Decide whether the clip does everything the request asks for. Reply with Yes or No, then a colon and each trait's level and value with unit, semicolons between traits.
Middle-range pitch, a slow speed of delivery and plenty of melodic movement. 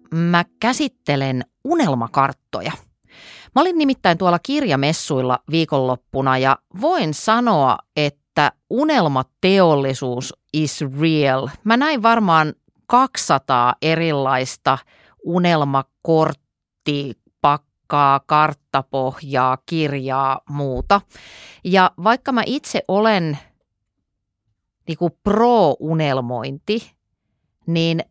Yes: medium, 150 Hz; slow, 75 wpm; wide, 5.8 semitones